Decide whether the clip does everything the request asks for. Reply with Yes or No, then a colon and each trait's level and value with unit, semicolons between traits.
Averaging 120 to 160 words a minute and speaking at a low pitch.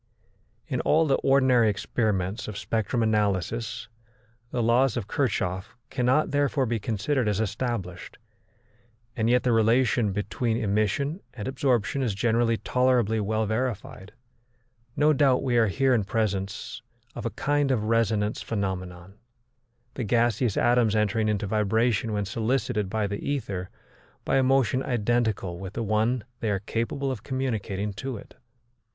Yes: average, 145 wpm; low, 115 Hz